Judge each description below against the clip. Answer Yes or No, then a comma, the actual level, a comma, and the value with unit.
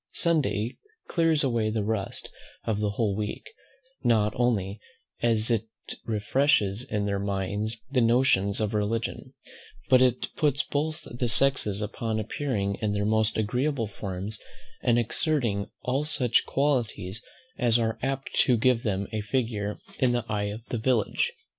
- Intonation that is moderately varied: Yes, average, 3.5 semitones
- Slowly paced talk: No, average, 150 wpm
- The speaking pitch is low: Yes, low, 110 Hz